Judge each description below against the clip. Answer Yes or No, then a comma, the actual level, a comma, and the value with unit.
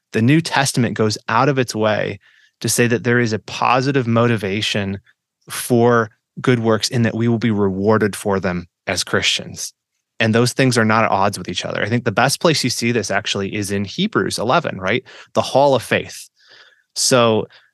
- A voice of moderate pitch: No, low, 115 Hz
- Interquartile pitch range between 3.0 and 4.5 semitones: No, narrow, 2.6 semitones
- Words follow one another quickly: No, average, 195 wpm